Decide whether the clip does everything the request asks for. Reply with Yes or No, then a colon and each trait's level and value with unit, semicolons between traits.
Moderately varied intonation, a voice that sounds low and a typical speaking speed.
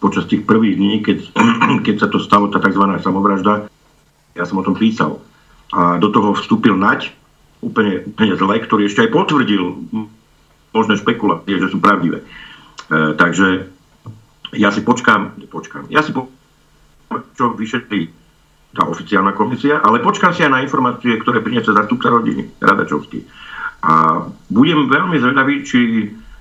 Yes: average, 3.1 semitones; low, 100 Hz; average, 145 wpm